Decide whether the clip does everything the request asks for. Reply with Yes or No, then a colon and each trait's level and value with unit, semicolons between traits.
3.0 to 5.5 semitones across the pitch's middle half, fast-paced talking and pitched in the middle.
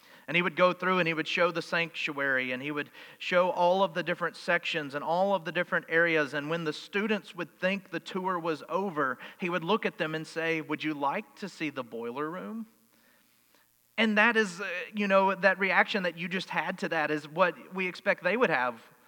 Yes: average, 3.4 semitones; fast, 225 wpm; medium, 175 Hz